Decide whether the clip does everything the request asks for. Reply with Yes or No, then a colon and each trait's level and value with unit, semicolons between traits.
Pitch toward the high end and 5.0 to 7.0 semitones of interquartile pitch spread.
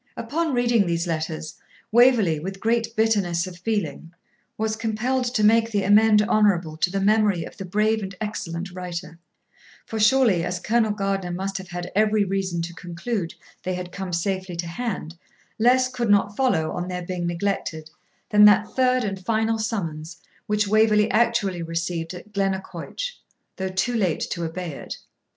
No: high, 195 Hz; average, 3.9 semitones